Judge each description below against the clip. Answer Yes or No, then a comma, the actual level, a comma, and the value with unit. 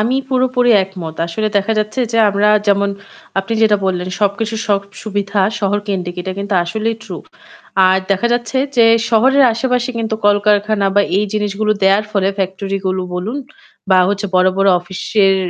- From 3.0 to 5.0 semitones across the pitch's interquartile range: No, narrow, 2.4 semitones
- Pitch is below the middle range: No, high, 205 Hz